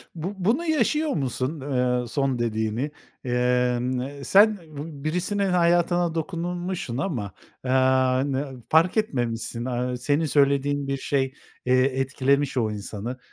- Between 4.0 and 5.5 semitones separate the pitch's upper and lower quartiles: Yes, average, 5.2 semitones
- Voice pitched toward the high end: No, medium, 140 Hz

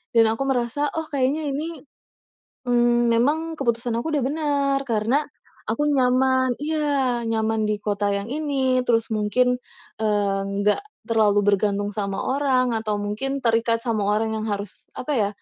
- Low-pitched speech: No, high, 240 Hz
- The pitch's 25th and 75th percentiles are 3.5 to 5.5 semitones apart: Yes, average, 4.3 semitones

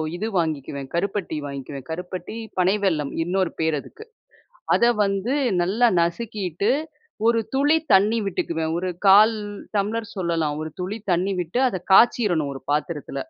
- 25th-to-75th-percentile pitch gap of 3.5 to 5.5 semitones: Yes, average, 4.6 semitones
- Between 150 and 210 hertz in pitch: Yes, medium, 185 Hz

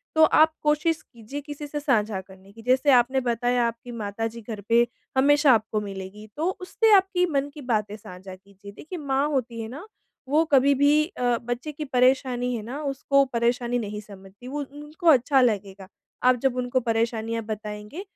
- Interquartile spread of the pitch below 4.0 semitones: No, average, 4.8 semitones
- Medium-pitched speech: No, high, 245 Hz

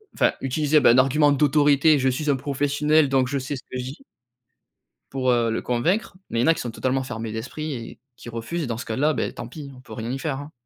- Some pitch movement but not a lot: Yes, average, 3.1 semitones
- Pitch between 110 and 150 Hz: Yes, low, 135 Hz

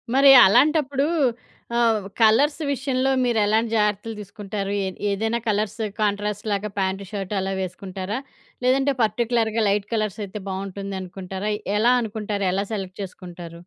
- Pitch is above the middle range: Yes, high, 210 Hz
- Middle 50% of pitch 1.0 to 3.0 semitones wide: Yes, average, 2.7 semitones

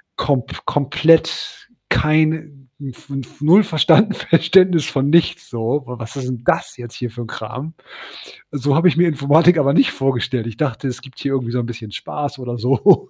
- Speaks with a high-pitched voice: No, medium, 140 Hz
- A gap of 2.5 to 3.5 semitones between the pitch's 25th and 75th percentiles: No, average, 4.4 semitones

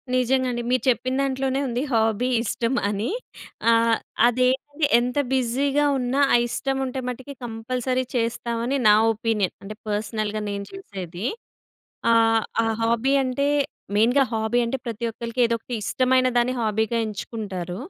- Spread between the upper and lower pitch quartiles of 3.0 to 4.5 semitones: No, narrow, 2.5 semitones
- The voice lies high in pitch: Yes, high, 235 Hz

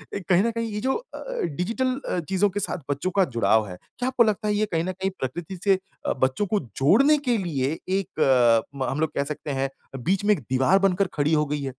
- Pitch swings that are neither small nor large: No, wide, 7.0 semitones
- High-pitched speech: No, medium, 180 Hz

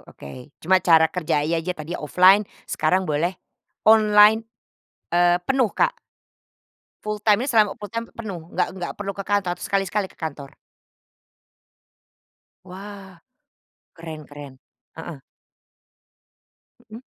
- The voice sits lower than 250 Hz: Yes, medium, 185 Hz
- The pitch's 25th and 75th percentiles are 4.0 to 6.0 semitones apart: Yes, average, 4.3 semitones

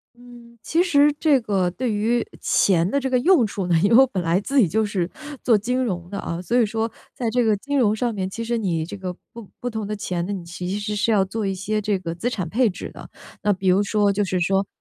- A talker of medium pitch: No, high, 210 Hz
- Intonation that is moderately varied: Yes, average, 4.0 semitones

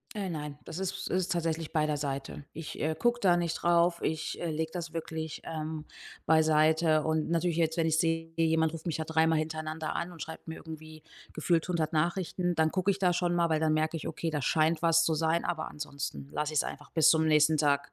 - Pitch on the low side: No, medium, 160 Hz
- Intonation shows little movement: Yes, narrow, 1.3 semitones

